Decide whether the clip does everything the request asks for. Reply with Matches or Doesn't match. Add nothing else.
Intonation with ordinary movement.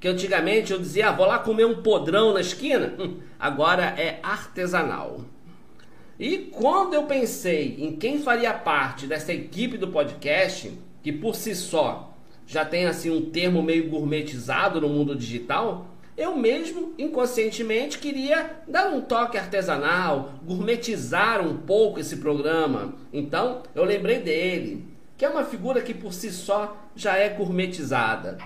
Doesn't match